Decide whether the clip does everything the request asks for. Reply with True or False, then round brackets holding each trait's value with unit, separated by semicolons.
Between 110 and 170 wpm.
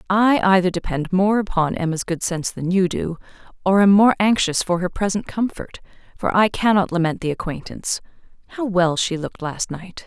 False (185 wpm)